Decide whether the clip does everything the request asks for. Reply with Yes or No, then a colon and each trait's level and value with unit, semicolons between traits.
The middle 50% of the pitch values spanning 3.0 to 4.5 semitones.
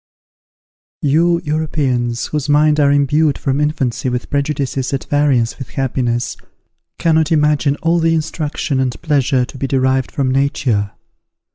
No: narrow, 2.6 semitones